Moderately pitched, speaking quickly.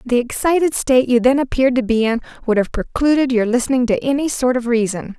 No: very high, 250 Hz; fast, 220 wpm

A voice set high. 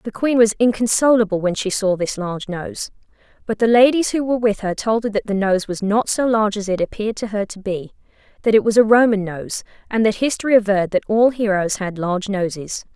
Yes: high, 210 Hz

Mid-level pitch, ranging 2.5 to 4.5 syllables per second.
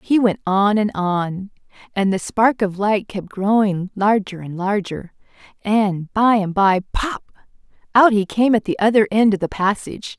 No: high, 205 Hz; 4.4 syllables/s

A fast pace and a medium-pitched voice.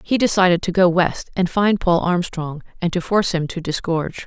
Yes: fast, 210 wpm; medium, 175 Hz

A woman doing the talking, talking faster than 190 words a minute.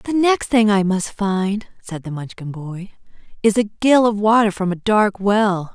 Yes: female; average, 200 wpm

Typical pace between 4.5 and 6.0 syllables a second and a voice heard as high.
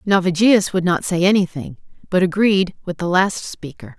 No: 4.9 syllables/s; medium, 180 Hz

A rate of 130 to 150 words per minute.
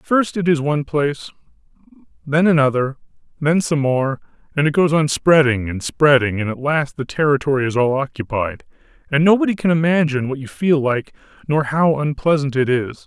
No: average, 175 wpm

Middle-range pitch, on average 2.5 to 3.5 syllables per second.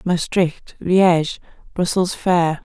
Yes: medium, 175 Hz; 3.2 syllables/s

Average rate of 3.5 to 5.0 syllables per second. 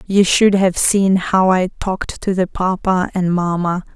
Yes: 4.1 syllables/s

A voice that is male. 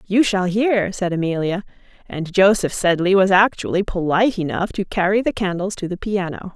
No: female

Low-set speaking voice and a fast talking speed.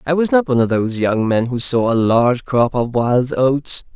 Yes: low, 125 Hz; fast, 245 wpm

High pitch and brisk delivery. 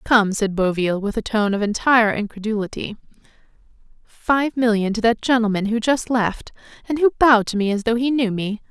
No: high, 225 Hz; average, 185 wpm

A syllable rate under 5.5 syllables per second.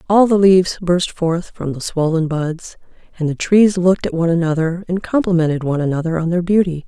No: 5.8 syllables/s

